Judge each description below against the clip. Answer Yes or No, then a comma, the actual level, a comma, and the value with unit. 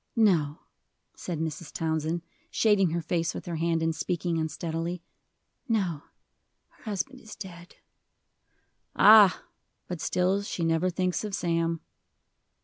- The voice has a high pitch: No, medium, 170 Hz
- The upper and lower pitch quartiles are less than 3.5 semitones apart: Yes, narrow, 2.5 semitones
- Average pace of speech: No, slow, 125 wpm